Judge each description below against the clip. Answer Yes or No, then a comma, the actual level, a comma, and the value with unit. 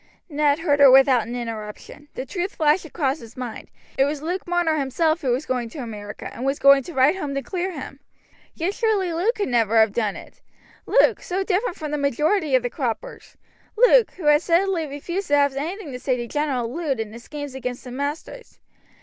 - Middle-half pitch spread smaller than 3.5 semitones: No, average, 5.3 semitones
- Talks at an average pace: No, fast, 210 wpm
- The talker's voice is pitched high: Yes, very high, 285 Hz